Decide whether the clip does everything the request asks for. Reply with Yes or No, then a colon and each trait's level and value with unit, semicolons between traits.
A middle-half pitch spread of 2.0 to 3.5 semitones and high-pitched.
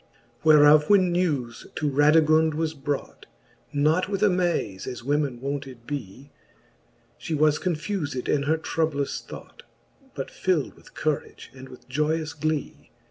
No: narrow, 2.5 semitones; medium, 150 Hz